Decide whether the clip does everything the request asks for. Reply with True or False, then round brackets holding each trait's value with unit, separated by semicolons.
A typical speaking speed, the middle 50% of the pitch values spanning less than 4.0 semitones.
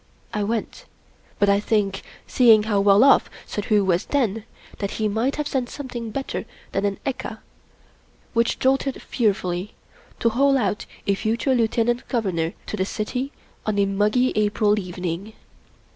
True (150 wpm; 3.6 semitones)